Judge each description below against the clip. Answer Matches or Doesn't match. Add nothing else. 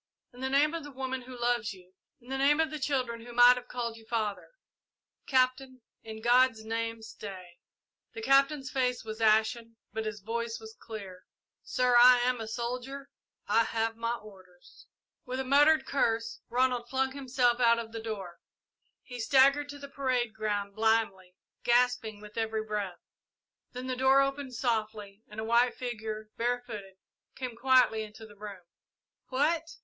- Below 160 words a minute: Doesn't match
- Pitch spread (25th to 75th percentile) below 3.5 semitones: Matches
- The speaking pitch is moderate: Doesn't match